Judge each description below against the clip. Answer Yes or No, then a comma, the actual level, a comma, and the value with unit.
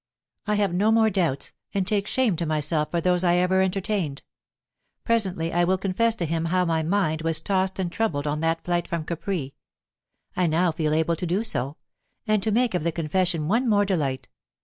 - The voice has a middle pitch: Yes, medium, 180 Hz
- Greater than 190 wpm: Yes, average, 200 wpm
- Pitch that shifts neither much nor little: Yes, average, 3.5 semitones